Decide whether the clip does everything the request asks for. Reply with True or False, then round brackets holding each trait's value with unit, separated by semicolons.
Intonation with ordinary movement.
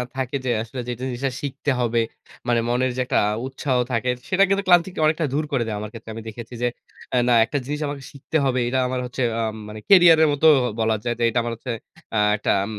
True (3.6 semitones)